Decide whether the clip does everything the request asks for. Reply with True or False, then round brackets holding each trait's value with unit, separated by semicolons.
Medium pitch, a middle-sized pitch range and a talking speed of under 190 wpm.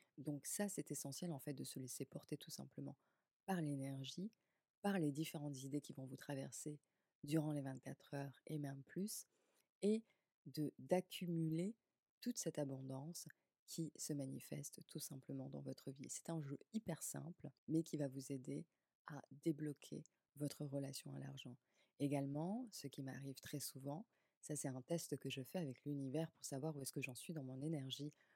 True (145 Hz; 3.2 semitones; 180 wpm)